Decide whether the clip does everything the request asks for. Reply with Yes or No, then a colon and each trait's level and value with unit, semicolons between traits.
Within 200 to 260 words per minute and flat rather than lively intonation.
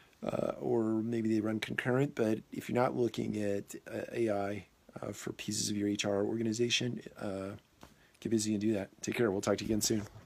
Yes: fast, 205 wpm; narrow, 1.9 semitones